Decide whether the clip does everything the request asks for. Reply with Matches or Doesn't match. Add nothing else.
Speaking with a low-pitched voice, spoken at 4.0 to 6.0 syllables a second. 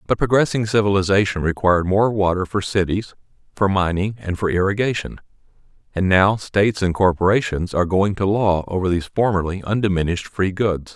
Matches